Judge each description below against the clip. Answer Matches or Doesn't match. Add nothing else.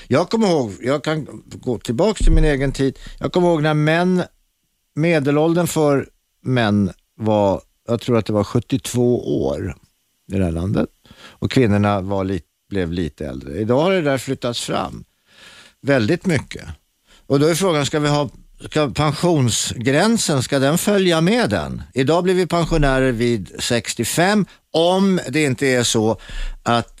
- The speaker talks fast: Doesn't match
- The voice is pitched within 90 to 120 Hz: Doesn't match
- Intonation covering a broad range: Matches